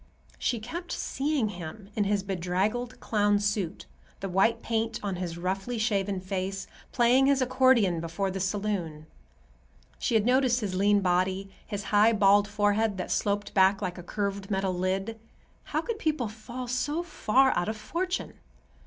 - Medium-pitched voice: No, high, 205 Hz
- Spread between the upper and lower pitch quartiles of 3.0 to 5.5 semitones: Yes, average, 3.5 semitones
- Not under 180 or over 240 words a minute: No, average, 160 wpm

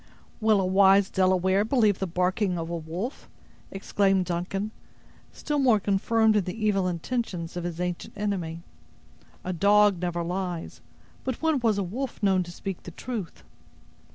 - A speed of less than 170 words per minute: Yes, average, 155 wpm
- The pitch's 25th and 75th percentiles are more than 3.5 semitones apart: No, average, 2.9 semitones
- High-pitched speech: Yes, high, 195 Hz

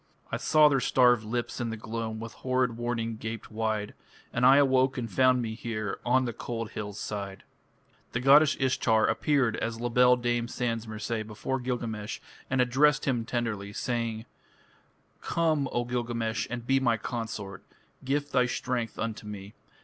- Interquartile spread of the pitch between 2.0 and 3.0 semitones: Yes, narrow, 2.4 semitones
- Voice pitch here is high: No, low, 120 Hz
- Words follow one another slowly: No, average, 165 wpm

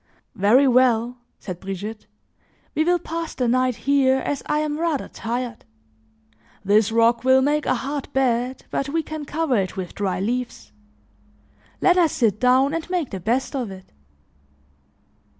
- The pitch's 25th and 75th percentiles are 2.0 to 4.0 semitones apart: No, average, 4.6 semitones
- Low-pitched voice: No, very high, 255 Hz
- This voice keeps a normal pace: Yes, average, 155 wpm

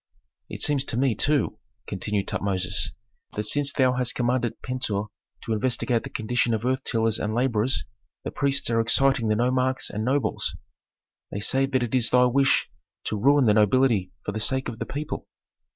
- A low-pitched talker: Yes, low, 120 Hz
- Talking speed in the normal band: Yes, average, 180 wpm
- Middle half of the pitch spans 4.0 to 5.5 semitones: No, average, 3.4 semitones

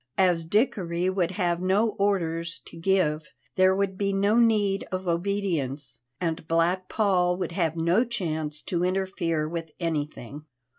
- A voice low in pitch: No, medium, 180 Hz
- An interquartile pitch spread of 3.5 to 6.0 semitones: No, average, 2.9 semitones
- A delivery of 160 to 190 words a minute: No, average, 145 wpm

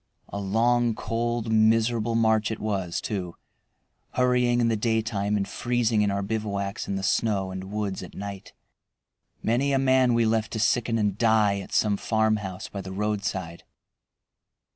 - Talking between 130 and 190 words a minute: Yes, average, 160 wpm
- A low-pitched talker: Yes, low, 110 Hz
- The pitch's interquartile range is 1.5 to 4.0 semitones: Yes, narrow, 2.6 semitones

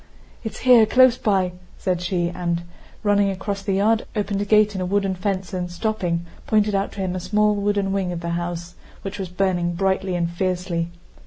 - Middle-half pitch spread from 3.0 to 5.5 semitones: No, narrow, 2.6 semitones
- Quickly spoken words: No, average, 195 wpm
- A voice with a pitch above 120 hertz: Yes, high, 190 Hz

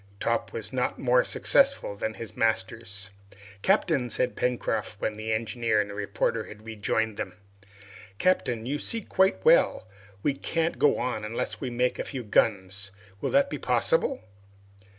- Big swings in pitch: No, average, 4.4 semitones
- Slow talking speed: No, average, 155 wpm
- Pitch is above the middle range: No, low, 115 Hz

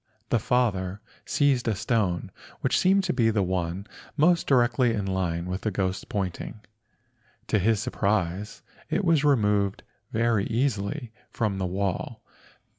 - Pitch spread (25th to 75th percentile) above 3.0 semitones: Yes, average, 4.4 semitones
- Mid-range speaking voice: No, low, 105 Hz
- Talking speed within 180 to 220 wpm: No, average, 145 wpm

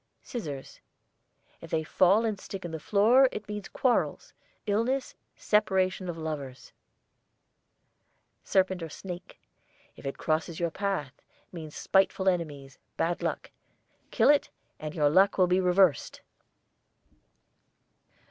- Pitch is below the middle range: No, medium, 180 Hz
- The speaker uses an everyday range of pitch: Yes, average, 4.0 semitones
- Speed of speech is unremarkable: No, slow, 120 wpm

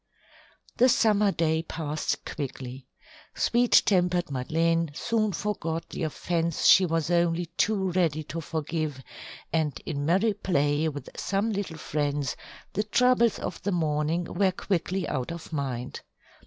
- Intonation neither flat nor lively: Yes, average, 4.1 semitones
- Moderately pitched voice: Yes, medium, 165 Hz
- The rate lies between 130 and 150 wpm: Yes, slow, 135 wpm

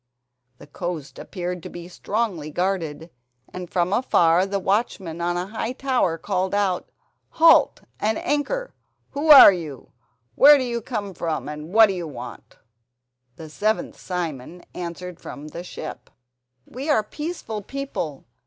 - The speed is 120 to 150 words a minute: Yes, average, 145 wpm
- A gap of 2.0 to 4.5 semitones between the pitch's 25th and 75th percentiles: No, average, 5.0 semitones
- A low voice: No, medium, 180 Hz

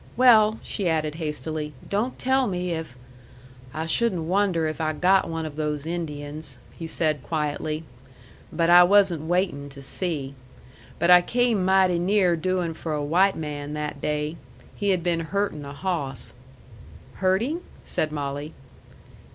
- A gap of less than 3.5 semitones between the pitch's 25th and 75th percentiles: No, average, 3.8 semitones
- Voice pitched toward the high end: No, medium, 165 Hz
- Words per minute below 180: Yes, average, 150 wpm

